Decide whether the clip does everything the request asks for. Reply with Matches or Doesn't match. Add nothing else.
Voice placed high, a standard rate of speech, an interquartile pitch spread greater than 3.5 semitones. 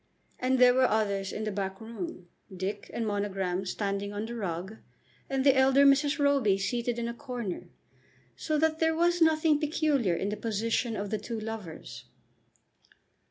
Matches